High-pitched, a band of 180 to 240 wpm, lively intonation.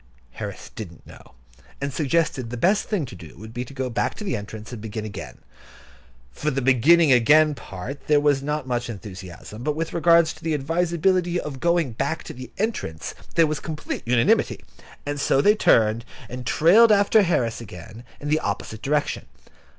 No: medium, 140 Hz; average, 190 wpm; wide, 6.0 semitones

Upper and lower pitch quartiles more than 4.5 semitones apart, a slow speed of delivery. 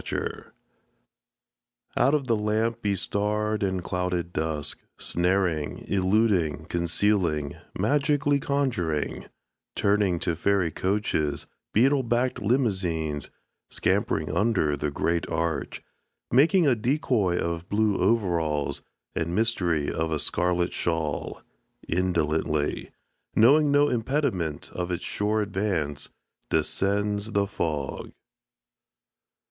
Yes: average, 5.2 semitones; slow, 100 wpm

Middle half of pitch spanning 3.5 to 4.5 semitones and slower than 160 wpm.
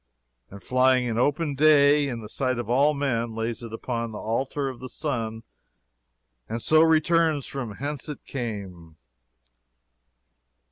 Yes: average, 4.1 semitones; average, 145 wpm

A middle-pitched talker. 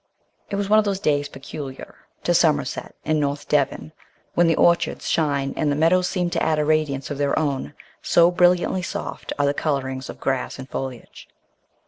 Yes: medium, 150 Hz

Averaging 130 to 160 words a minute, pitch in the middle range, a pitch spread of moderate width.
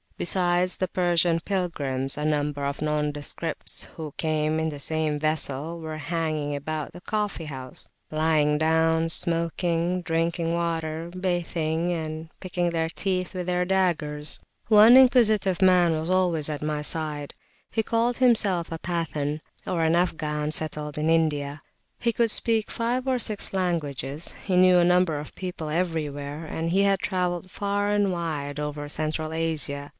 Yes: average, 150 wpm; medium, 165 Hz; average, 3.1 semitones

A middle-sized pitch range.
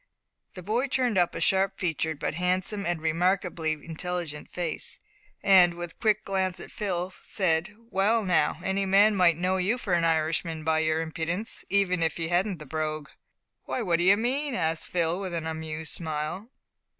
Yes: average, 3.3 semitones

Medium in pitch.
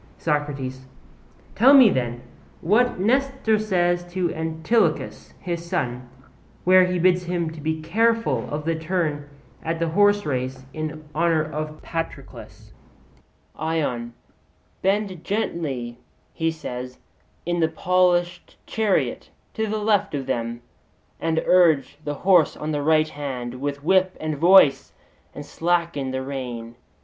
Yes: medium, 160 Hz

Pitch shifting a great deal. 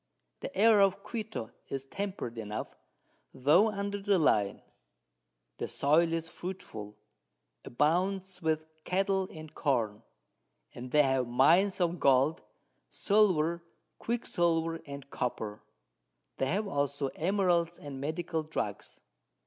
Yes: wide, 5.8 semitones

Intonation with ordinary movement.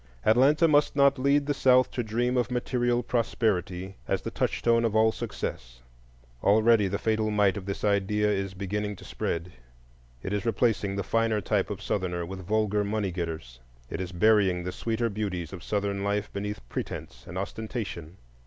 Yes: average, 3.3 semitones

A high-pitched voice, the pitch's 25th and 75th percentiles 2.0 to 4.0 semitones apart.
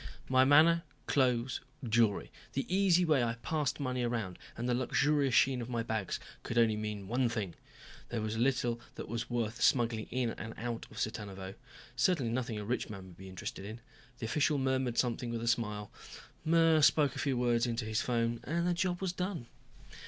No: low, 120 Hz; average, 2.9 semitones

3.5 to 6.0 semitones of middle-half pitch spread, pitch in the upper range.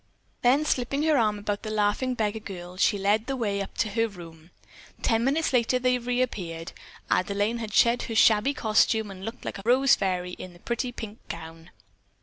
Yes: average, 3.8 semitones; high, 220 Hz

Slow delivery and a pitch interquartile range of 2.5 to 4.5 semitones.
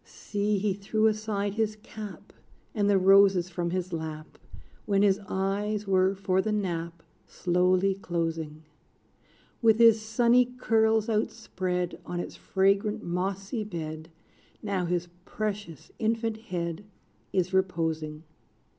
Yes: slow, 120 wpm; average, 3.3 semitones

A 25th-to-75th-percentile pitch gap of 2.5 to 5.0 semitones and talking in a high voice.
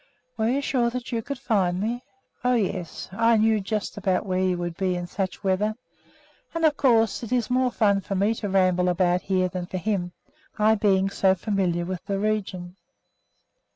Yes: average, 3.4 semitones; high, 195 Hz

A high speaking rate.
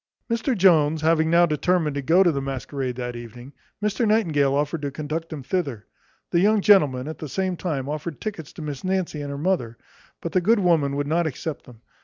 Yes: fast, 210 wpm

